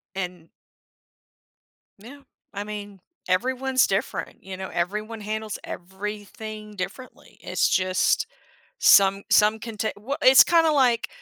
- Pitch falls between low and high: No, high, 210 Hz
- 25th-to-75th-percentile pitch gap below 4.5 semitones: Yes, average, 3.3 semitones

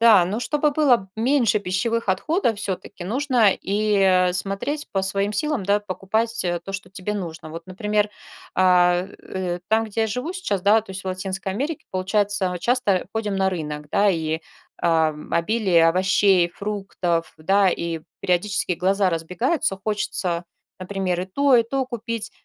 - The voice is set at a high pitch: Yes, high, 195 Hz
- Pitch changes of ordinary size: Yes, average, 3.5 semitones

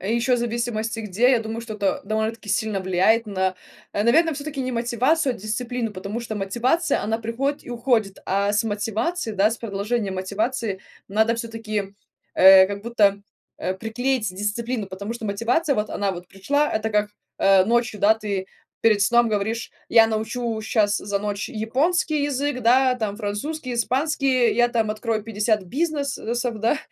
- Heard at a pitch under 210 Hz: No, high, 225 Hz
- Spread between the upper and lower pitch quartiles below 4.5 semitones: Yes, average, 2.9 semitones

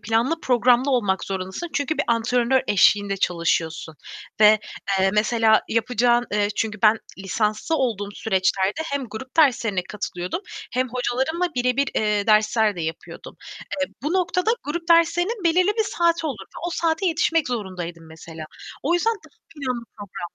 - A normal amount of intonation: No, wide, 7.5 semitones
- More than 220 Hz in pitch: Yes, high, 235 Hz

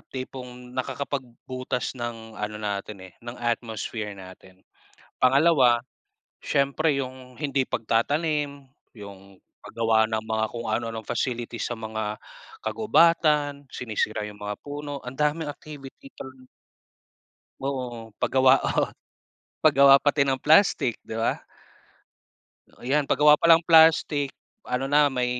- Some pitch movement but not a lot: Yes, average, 4.2 semitones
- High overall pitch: No, low, 130 Hz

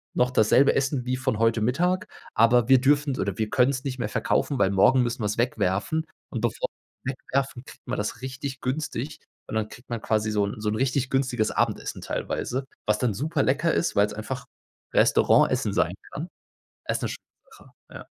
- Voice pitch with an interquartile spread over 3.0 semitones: Yes, average, 3.8 semitones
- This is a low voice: Yes, low, 125 Hz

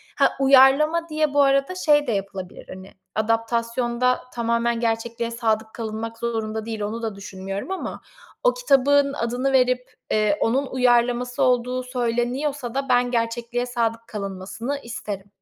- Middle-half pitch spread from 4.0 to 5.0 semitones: No, average, 2.8 semitones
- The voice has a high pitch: Yes, high, 240 Hz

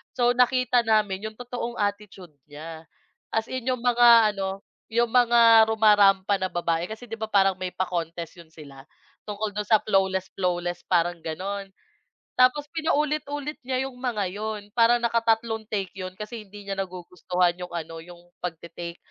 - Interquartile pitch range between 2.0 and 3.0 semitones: No, average, 4.6 semitones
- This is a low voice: No, high, 205 Hz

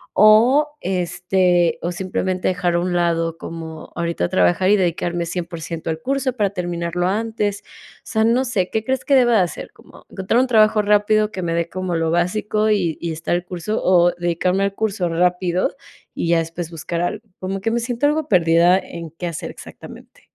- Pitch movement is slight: No, average, 3.8 semitones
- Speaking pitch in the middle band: Yes, medium, 180 Hz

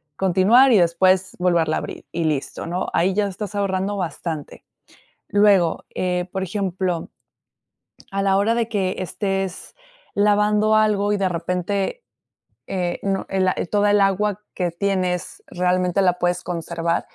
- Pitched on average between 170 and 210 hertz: Yes, high, 190 Hz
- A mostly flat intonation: Yes, narrow, 2.3 semitones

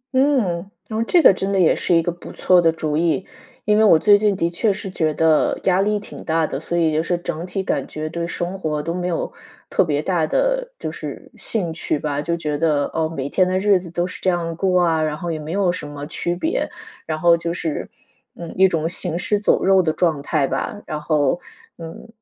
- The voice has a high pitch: No, medium, 170 Hz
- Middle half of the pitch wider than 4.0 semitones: No, average, 3.1 semitones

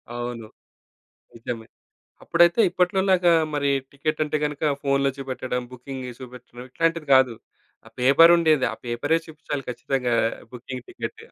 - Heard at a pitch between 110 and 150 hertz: Yes, medium, 140 Hz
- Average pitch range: Yes, average, 4.8 semitones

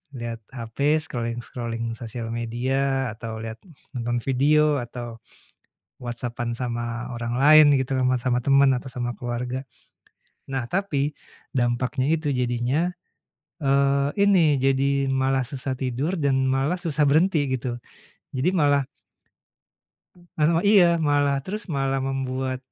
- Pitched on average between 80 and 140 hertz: Yes, low, 135 Hz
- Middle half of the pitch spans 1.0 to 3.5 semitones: Yes, average, 3.0 semitones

